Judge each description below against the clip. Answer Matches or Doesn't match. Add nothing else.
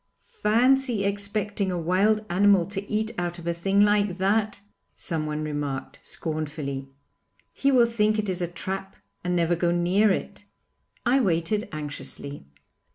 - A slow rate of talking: Doesn't match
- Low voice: Doesn't match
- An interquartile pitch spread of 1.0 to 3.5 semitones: Doesn't match